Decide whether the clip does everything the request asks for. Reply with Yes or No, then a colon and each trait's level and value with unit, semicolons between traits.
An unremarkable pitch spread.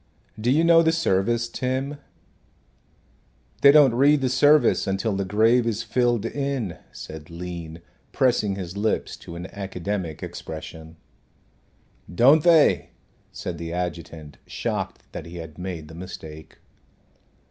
No: wide, 7.3 semitones